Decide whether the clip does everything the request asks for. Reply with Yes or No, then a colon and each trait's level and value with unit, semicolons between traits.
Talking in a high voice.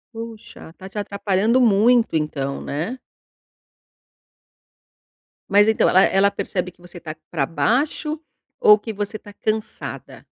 Yes: high, 205 Hz